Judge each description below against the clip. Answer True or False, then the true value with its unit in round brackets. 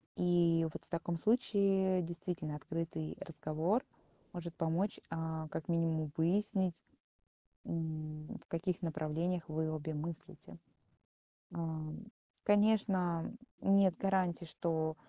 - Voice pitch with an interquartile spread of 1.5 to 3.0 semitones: True (2.6 semitones)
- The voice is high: False (165 Hz)